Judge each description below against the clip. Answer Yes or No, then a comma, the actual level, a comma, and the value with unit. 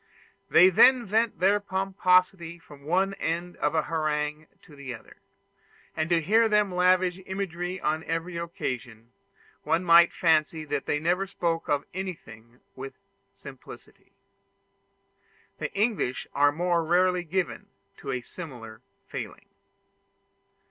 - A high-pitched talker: No, medium, 170 Hz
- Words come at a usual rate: No, slow, 125 wpm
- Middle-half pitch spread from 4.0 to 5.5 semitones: No, average, 3.5 semitones